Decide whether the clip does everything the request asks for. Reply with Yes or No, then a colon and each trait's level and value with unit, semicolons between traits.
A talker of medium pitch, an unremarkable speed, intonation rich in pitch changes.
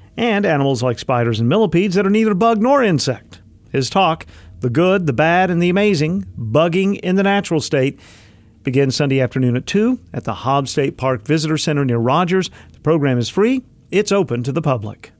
Yes: medium, 150 Hz; average, 195 wpm; wide, 7.2 semitones